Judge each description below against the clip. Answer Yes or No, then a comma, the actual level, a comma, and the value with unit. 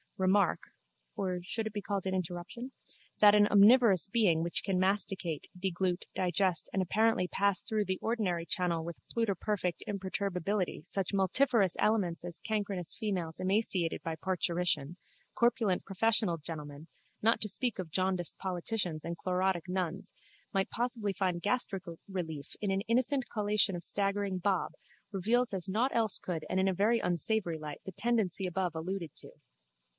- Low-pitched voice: No, high, 190 Hz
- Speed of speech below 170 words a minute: Yes, average, 150 wpm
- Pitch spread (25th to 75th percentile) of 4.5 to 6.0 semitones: No, average, 3.0 semitones